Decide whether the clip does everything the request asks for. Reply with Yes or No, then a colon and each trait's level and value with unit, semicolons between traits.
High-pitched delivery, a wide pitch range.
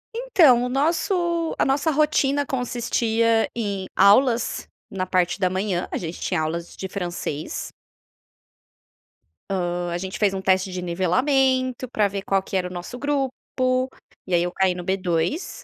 Yes: high, 200 Hz; wide, 6.5 semitones